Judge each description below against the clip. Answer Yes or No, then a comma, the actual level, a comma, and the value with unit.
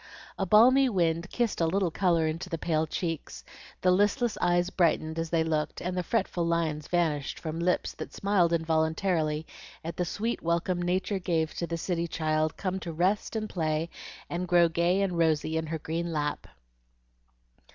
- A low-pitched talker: No, medium, 170 Hz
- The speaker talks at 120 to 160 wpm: No, average, 170 wpm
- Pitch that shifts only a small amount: Yes, narrow, 2.3 semitones